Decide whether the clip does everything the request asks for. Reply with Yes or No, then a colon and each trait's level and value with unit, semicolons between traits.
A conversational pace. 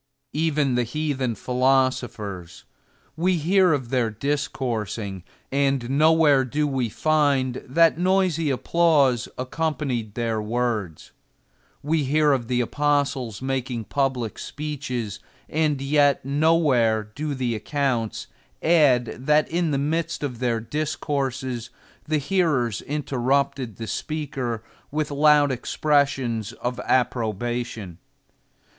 No: slow, 110 wpm